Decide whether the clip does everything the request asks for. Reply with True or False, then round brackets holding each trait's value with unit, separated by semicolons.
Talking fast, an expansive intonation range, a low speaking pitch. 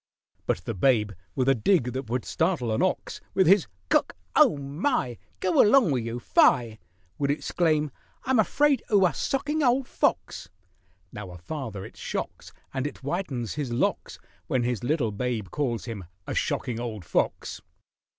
False (165 wpm; 7.3 semitones; 130 Hz)